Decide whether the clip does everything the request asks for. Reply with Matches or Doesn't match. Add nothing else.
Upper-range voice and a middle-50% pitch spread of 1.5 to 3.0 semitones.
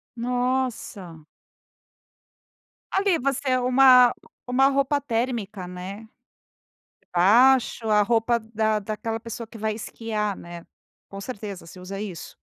Doesn't match